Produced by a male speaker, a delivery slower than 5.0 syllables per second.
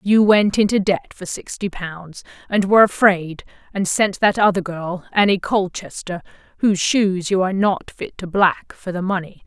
No: female; 4.7 syllables/s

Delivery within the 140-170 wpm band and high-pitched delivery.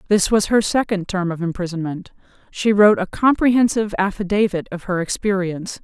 Yes: average, 155 wpm; high, 195 Hz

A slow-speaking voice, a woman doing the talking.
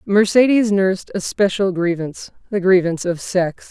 Yes: slow, 130 wpm; female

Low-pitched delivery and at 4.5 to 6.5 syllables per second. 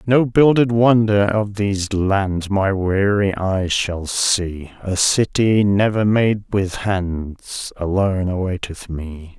No: low, 100 Hz; 3.3 syllables/s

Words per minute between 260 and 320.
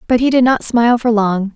Yes: fast, 270 wpm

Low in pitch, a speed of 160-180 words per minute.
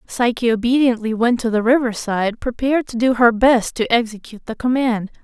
No: high, 235 Hz; average, 170 wpm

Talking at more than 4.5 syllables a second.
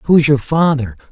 No: 4.2 syllables/s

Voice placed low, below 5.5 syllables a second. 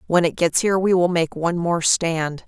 No: medium, 170 Hz; 5.2 syllables/s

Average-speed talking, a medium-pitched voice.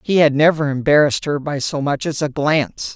No: fast, 225 wpm; medium, 145 Hz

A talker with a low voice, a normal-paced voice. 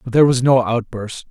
No: low, 120 Hz; fast, 230 wpm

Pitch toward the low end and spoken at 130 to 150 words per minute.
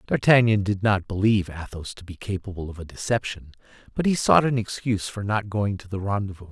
No: low, 100 Hz; average, 200 wpm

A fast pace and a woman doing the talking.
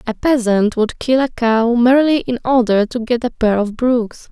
Yes: fast, 210 wpm; female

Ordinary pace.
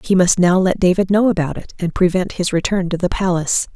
No: fast, 240 wpm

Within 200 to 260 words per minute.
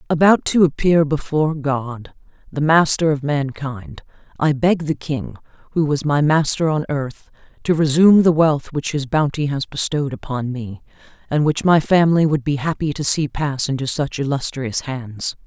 No: average, 170 wpm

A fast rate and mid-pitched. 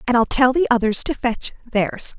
No: fast, 220 wpm; high, 240 Hz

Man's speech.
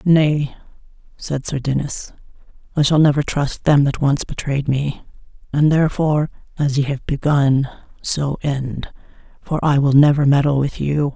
No: female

